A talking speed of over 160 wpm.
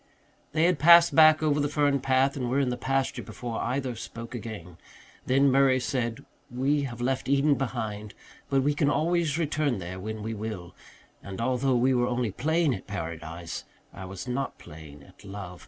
Yes: average, 185 wpm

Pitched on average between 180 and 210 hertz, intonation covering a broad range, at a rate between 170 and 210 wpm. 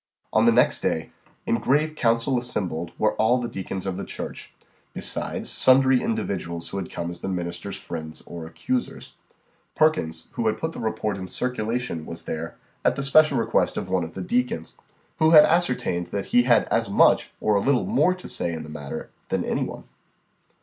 No: low, 110 Hz; wide, 7.3 semitones; average, 190 wpm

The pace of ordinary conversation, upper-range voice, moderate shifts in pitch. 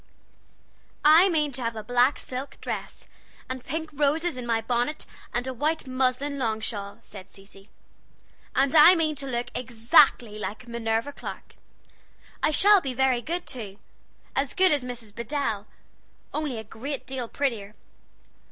Yes: average, 150 wpm; very high, 255 Hz; average, 4.3 semitones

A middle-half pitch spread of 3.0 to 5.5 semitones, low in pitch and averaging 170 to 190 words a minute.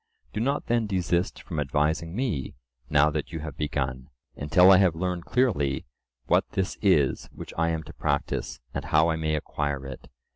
Yes: average, 3.9 semitones; very low, 80 Hz; average, 180 wpm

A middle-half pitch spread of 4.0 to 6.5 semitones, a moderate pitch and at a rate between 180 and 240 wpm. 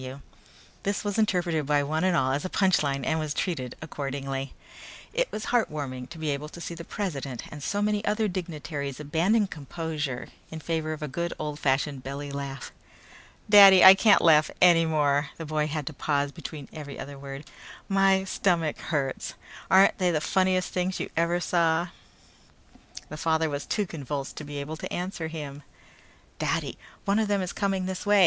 Yes: average, 4.5 semitones; medium, 160 Hz; average, 185 wpm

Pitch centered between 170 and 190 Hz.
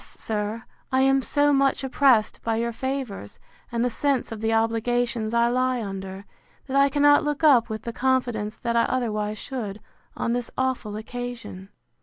No: high, 235 Hz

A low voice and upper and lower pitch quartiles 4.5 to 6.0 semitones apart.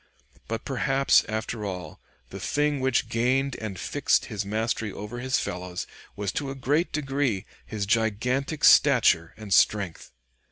Yes: low, 115 Hz; average, 4.9 semitones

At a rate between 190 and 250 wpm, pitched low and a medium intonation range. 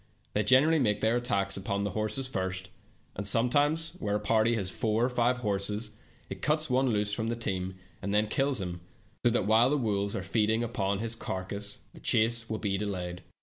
Yes: average, 200 wpm; low, 110 Hz; average, 3.3 semitones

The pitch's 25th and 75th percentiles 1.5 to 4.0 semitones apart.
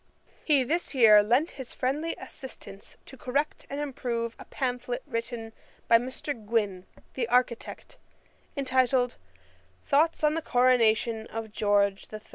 Yes: average, 3.0 semitones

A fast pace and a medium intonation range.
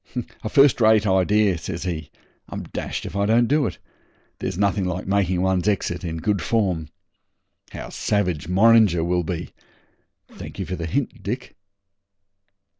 No: average, 155 wpm; average, 3.7 semitones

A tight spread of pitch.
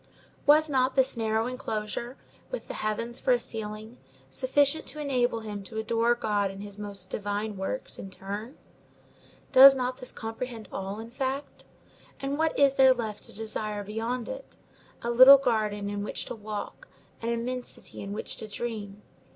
No: average, 3.5 semitones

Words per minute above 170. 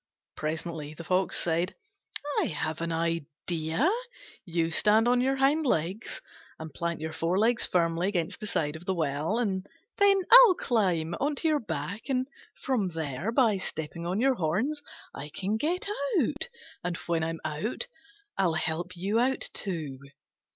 No: average, 160 wpm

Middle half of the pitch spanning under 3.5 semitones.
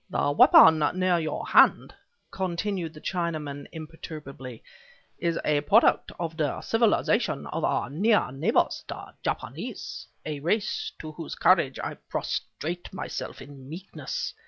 No: average, 3.9 semitones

